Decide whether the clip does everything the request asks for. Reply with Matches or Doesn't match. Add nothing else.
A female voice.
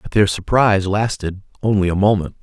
Doesn't match